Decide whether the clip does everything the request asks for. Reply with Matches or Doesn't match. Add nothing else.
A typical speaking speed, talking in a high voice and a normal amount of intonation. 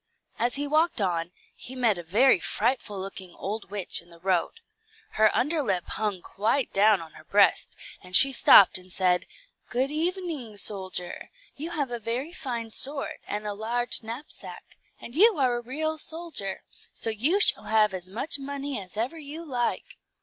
Doesn't match